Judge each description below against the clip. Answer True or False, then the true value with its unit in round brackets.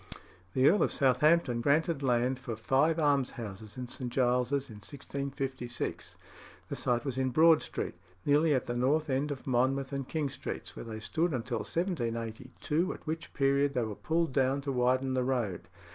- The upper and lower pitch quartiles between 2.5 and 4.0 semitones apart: True (2.9 semitones)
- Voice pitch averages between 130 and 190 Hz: True (135 Hz)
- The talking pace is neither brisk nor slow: True (175 wpm)